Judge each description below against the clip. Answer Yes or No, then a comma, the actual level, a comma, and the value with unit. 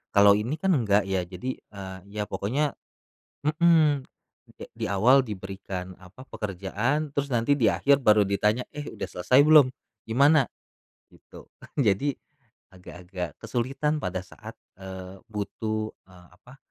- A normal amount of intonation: No, wide, 6.4 semitones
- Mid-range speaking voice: No, low, 110 Hz